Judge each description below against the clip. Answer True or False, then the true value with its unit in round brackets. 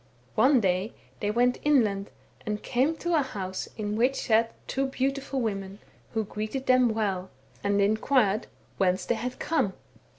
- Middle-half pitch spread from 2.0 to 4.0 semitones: False (4.5 semitones)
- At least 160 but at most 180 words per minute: False (190 wpm)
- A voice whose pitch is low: False (220 Hz)